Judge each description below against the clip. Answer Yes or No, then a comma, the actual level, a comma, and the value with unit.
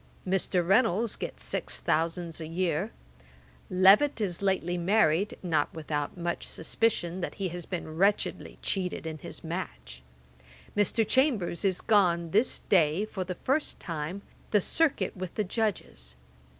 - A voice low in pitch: No, medium, 180 Hz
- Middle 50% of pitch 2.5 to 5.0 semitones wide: Yes, average, 3.8 semitones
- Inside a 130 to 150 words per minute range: Yes, average, 140 wpm